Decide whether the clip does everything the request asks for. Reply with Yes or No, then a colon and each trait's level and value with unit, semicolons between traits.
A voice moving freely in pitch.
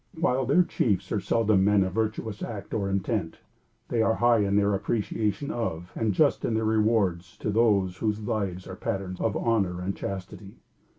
No: average, 2.7 semitones